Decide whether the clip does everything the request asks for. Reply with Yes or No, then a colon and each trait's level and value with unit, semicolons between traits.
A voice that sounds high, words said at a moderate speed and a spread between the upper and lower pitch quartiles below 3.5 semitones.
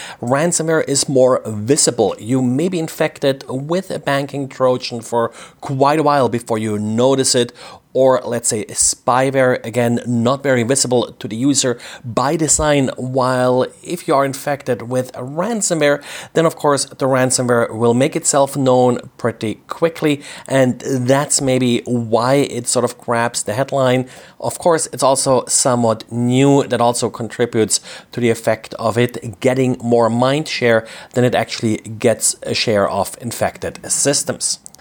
No: low, 130 Hz; average, 155 wpm; average, 2.8 semitones